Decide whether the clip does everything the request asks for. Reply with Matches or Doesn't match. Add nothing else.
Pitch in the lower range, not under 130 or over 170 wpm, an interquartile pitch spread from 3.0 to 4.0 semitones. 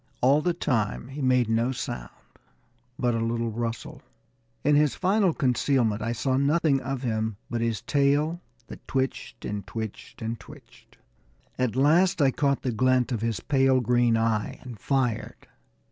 Matches